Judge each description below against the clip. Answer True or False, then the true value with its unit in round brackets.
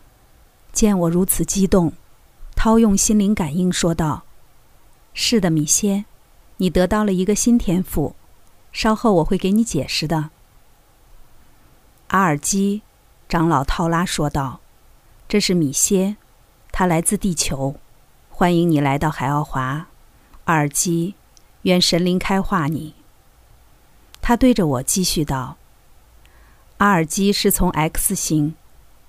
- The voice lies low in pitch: False (170 Hz)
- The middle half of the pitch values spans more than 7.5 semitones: False (5.1 semitones)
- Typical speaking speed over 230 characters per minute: False (175 characters per minute)